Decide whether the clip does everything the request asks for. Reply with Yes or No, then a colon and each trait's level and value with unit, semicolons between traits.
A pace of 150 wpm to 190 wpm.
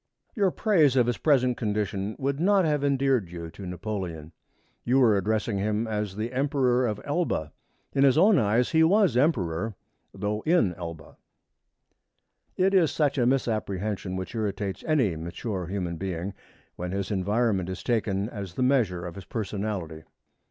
Yes: average, 160 wpm